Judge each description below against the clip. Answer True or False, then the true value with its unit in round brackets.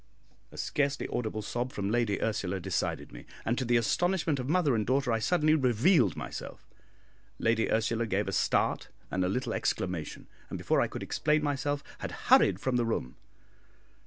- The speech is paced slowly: False (175 wpm)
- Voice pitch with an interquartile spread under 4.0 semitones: False (4.8 semitones)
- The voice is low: True (120 Hz)